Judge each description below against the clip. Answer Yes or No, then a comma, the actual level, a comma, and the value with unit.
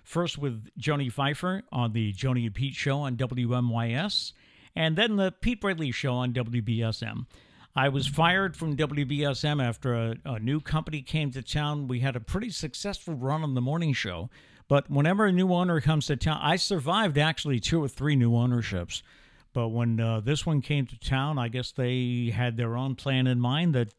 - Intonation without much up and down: No, average, 4.3 semitones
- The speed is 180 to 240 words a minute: Yes, average, 195 wpm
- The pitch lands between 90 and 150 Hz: Yes, low, 135 Hz